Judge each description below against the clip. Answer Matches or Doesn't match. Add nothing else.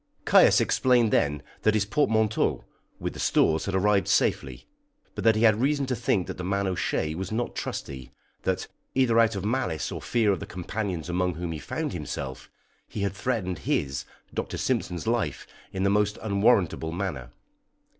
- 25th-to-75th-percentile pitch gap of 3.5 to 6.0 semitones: Matches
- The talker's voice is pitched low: Matches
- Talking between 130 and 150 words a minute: Doesn't match